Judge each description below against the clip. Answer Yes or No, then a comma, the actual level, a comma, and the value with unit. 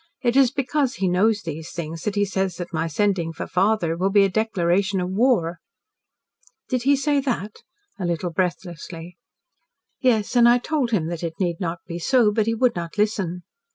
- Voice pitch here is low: No, high, 195 Hz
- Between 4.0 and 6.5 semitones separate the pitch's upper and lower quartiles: Yes, average, 4.9 semitones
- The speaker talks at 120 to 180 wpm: No, average, 190 wpm